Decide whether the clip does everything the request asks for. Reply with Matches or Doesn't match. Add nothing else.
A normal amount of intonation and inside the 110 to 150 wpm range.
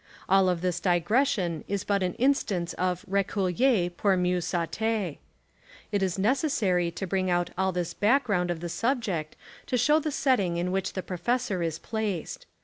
Doesn't match